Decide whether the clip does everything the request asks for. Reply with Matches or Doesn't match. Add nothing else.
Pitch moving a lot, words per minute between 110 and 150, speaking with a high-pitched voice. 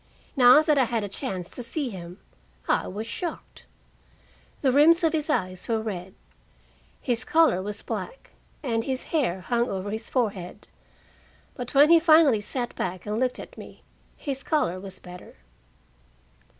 Doesn't match